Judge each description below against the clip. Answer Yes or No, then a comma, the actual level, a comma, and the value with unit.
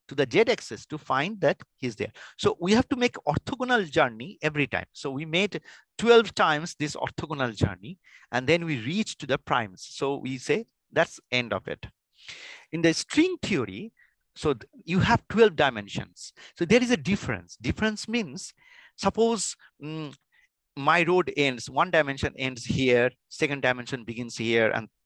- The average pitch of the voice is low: No, medium, 155 Hz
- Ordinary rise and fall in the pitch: No, wide, 8.0 semitones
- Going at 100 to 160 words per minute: No, average, 170 wpm